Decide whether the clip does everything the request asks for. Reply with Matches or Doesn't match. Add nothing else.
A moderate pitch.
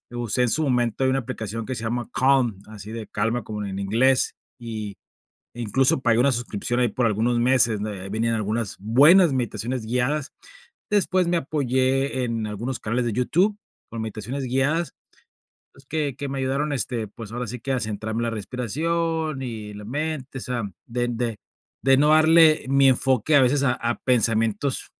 Doesn't match